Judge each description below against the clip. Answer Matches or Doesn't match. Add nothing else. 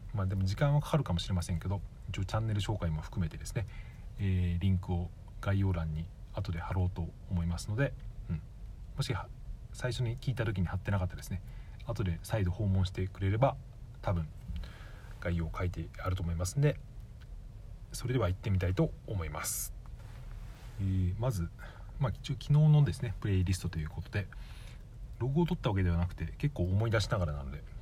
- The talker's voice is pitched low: Matches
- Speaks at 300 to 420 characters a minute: Matches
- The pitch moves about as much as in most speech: Matches